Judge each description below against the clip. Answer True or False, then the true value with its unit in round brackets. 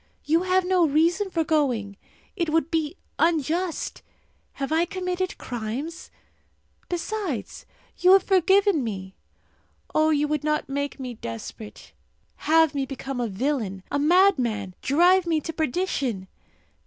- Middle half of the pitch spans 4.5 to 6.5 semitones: True (5.3 semitones)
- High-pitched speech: True (310 Hz)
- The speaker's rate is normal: False (130 wpm)